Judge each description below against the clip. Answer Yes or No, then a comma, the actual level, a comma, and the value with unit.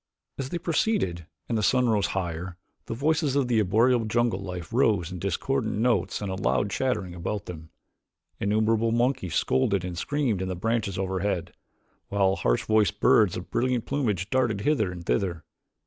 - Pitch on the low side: Yes, low, 105 Hz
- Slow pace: No, average, 165 wpm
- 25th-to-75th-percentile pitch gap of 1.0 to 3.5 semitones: No, average, 4.7 semitones